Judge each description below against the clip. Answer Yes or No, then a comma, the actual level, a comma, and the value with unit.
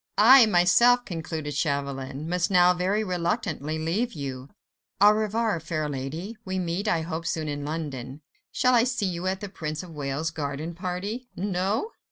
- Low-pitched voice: No, medium, 175 Hz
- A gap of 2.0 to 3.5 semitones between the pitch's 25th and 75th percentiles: No, average, 4.9 semitones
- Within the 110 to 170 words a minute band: Yes, average, 160 wpm